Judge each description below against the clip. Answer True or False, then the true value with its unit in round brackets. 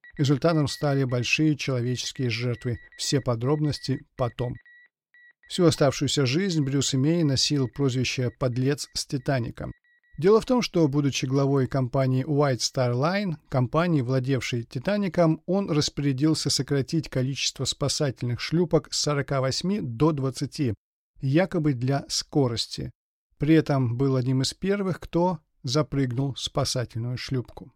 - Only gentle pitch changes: False (3.4 semitones)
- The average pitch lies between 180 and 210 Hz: False (140 Hz)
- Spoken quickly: False (120 wpm)